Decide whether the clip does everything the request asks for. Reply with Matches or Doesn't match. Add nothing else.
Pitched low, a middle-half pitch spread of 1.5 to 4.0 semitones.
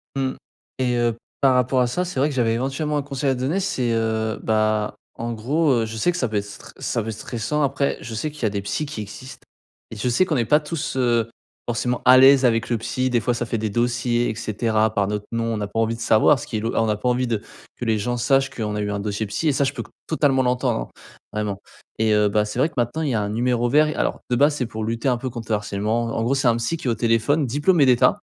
Matches